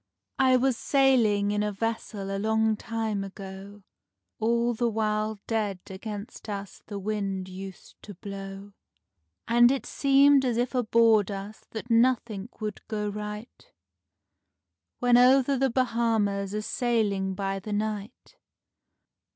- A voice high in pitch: Yes, high, 215 Hz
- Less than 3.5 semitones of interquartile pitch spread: Yes, average, 2.9 semitones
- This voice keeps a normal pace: No, slow, 130 wpm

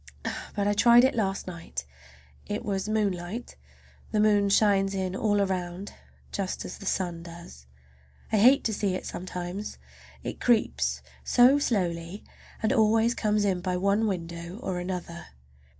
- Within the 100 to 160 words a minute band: Yes, average, 150 wpm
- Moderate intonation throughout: Yes, average, 3.1 semitones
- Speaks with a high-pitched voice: Yes, high, 195 Hz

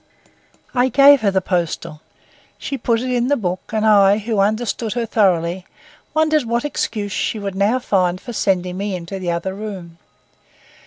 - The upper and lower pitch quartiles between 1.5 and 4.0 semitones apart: No, average, 4.4 semitones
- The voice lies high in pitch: Yes, high, 205 Hz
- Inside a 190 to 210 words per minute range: No, average, 170 wpm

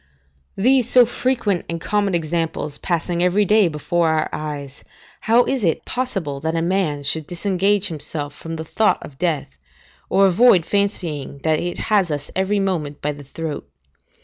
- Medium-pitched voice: Yes, medium, 170 Hz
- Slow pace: No, average, 160 wpm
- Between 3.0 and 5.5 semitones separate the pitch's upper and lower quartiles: Yes, average, 4.8 semitones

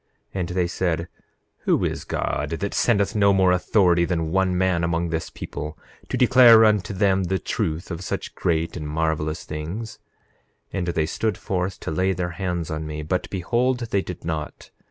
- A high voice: No, very low, 90 Hz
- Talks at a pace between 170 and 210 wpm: Yes, average, 185 wpm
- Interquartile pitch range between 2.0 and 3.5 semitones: Yes, average, 3.1 semitones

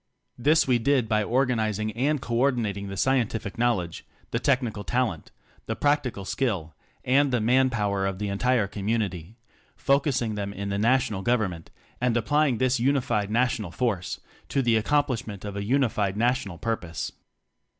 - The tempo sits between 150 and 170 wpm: Yes, average, 160 wpm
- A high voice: No, low, 115 Hz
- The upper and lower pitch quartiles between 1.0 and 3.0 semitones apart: No, average, 4.1 semitones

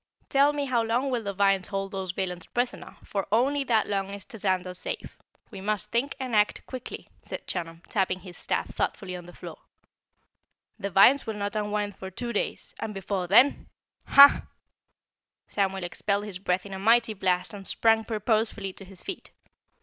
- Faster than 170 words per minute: Yes, average, 180 wpm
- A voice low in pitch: No, high, 205 Hz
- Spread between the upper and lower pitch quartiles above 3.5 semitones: No, average, 3.1 semitones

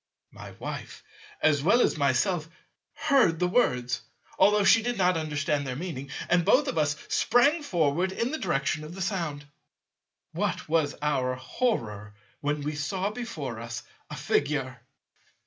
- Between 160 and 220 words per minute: No, average, 150 wpm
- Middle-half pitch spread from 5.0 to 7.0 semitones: Yes, average, 5.3 semitones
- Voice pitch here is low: No, medium, 155 Hz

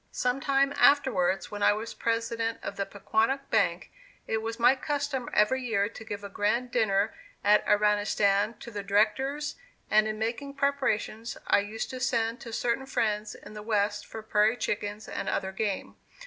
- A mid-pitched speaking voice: No, high, 220 Hz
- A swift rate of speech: No, average, 170 wpm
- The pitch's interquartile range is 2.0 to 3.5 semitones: Yes, average, 3.2 semitones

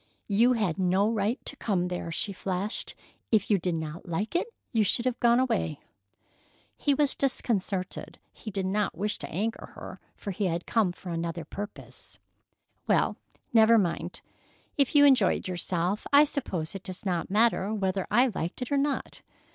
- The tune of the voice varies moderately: Yes, average, 4.5 semitones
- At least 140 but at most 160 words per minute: No, average, 170 wpm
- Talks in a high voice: Yes, high, 205 Hz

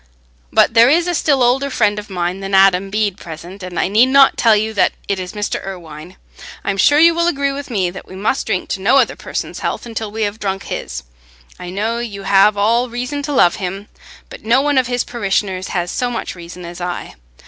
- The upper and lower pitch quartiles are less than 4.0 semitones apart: No, average, 4.6 semitones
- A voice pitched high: Yes, high, 205 Hz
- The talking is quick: Yes, fast, 225 wpm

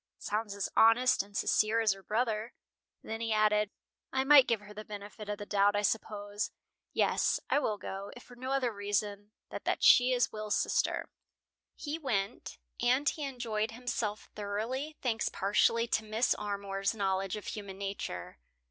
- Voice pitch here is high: Yes, high, 215 Hz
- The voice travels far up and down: No, average, 2.9 semitones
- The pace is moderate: Yes, average, 170 wpm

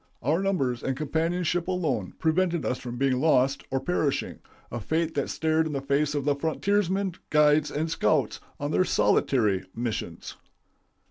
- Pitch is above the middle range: No, medium, 150 Hz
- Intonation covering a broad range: No, average, 3.8 semitones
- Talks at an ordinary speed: Yes, average, 150 wpm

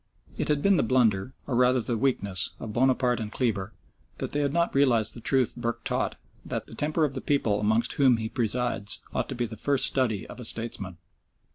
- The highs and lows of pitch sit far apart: No, average, 3.3 semitones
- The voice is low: Yes, low, 120 Hz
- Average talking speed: No, fast, 215 wpm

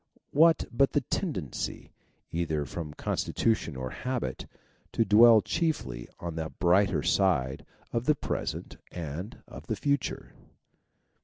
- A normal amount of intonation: No, wide, 8.1 semitones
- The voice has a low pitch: Yes, low, 100 Hz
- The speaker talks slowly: Yes, slow, 130 wpm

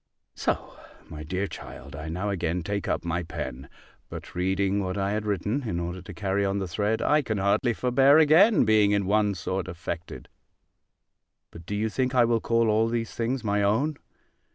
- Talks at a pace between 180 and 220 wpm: Yes, average, 190 wpm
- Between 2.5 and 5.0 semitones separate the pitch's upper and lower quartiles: Yes, average, 3.8 semitones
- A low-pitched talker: Yes, low, 100 Hz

